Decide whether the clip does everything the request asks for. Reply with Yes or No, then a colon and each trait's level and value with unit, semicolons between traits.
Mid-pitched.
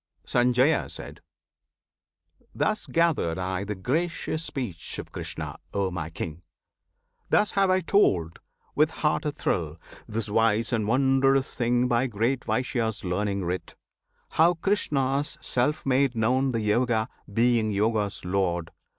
No: low, 120 Hz